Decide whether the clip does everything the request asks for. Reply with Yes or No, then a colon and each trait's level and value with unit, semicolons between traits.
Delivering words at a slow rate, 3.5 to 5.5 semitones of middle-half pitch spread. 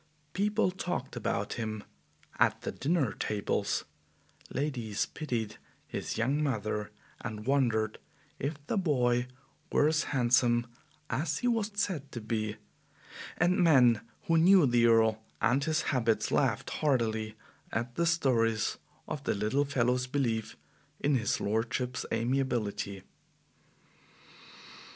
Yes: slow, 120 wpm; average, 4.9 semitones